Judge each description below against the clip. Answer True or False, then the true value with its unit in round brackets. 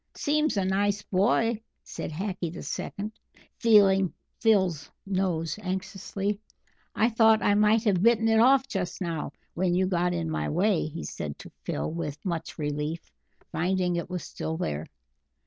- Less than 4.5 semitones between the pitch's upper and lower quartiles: True (3.8 semitones)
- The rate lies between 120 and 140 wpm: False (155 wpm)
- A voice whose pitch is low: False (190 Hz)